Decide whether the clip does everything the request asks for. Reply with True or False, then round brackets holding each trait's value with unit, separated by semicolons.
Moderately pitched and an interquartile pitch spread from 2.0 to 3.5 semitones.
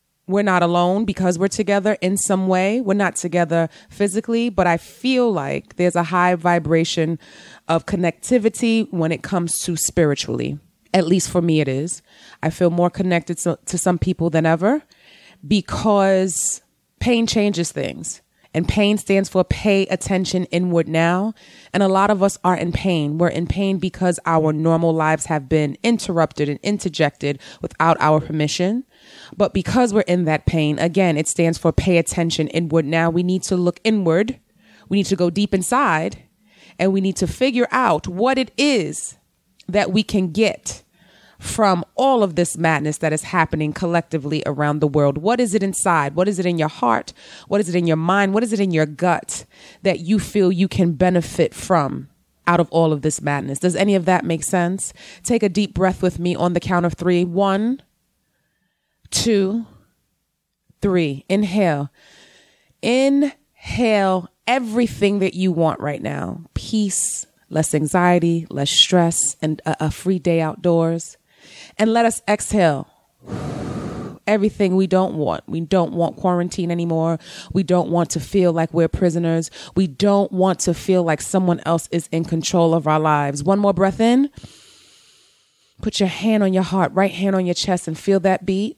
True (180 Hz; 3.2 semitones)